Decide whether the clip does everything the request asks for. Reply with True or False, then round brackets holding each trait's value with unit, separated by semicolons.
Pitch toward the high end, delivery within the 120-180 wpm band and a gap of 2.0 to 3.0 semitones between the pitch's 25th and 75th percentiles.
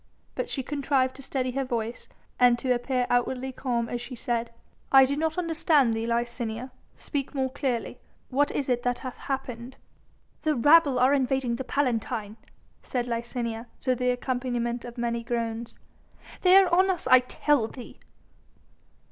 True (250 Hz; 160 wpm; 2.4 semitones)